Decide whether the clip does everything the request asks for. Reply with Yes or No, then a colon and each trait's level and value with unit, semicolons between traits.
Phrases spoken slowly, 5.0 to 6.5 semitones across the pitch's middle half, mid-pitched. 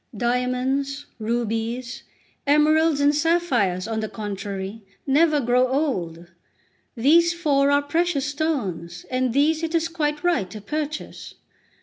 No: slow, 120 wpm; average, 5.3 semitones; very high, 275 Hz